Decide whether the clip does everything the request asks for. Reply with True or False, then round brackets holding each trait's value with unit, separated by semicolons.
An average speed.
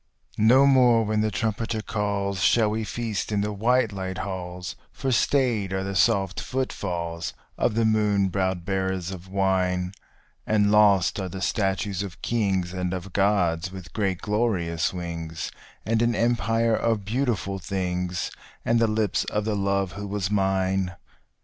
True (155 wpm)